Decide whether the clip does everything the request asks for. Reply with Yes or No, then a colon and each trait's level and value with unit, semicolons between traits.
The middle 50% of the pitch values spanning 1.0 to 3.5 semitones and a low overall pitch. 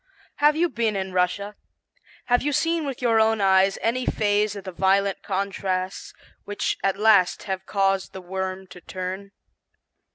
No: average, 2.7 semitones; high, 200 Hz